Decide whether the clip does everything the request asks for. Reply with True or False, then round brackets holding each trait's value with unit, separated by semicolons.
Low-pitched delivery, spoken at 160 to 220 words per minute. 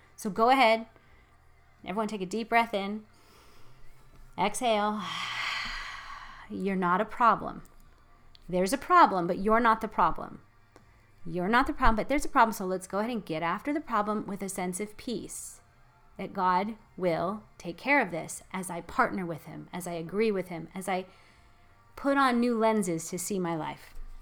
False (195 Hz; 175 wpm)